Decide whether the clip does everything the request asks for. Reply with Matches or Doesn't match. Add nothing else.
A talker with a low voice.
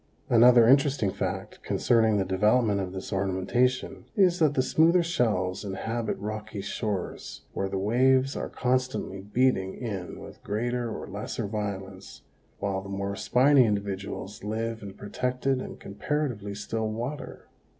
Matches